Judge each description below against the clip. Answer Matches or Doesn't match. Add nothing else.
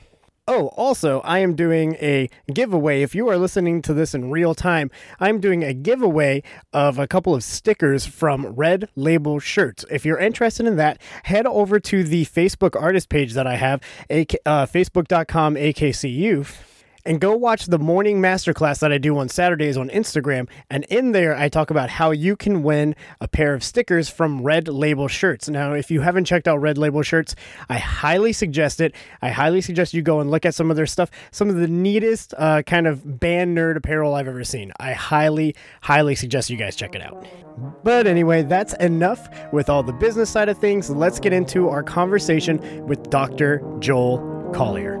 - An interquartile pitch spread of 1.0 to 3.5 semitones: Doesn't match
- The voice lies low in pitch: Doesn't match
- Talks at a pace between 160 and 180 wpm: Doesn't match